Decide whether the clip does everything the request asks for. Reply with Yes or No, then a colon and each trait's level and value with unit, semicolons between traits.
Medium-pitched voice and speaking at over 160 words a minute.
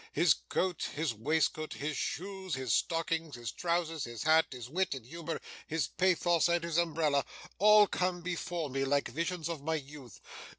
Yes: medium, 160 Hz; average, 170 wpm